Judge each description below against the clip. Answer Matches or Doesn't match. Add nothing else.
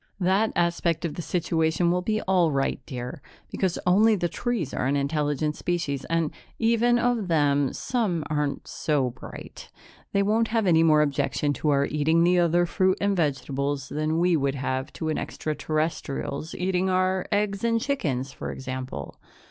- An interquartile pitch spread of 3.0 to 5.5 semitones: Matches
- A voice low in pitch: Doesn't match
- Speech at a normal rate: Matches